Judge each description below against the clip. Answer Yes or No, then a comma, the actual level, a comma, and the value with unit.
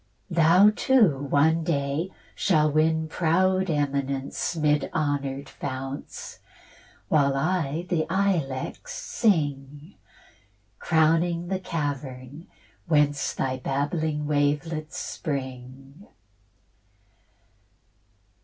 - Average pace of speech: No, slow, 80 wpm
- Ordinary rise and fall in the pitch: Yes, average, 3.2 semitones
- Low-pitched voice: No, medium, 150 Hz